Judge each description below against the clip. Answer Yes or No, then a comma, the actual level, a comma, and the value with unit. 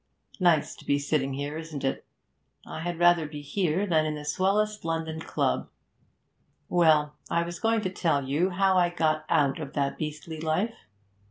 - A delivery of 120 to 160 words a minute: No, average, 175 wpm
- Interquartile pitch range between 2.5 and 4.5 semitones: Yes, average, 2.9 semitones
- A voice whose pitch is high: No, medium, 160 Hz